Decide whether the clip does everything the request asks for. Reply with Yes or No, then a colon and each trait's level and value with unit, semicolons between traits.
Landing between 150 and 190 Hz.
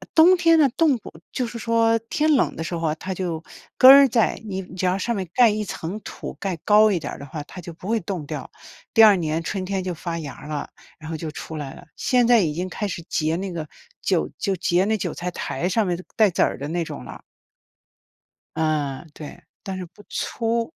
Yes: medium, 185 Hz